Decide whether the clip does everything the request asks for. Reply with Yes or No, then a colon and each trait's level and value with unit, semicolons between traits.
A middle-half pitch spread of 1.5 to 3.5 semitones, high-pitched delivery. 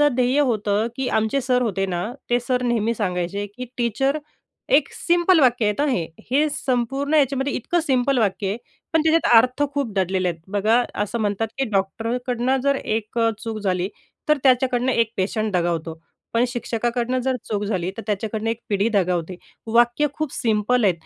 No: average, 4.1 semitones; high, 235 Hz